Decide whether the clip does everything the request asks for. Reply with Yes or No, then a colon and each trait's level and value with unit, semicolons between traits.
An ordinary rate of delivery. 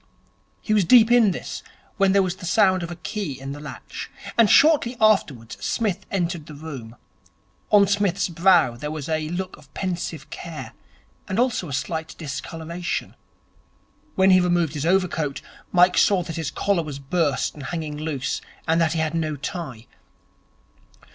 Yes: average, 165 wpm